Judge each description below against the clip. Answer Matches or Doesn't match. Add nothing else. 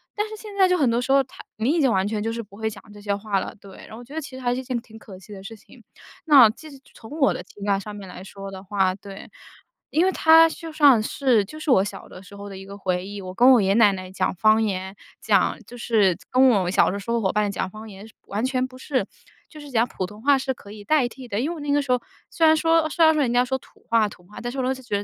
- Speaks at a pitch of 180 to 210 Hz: Doesn't match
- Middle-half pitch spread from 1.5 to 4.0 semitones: Doesn't match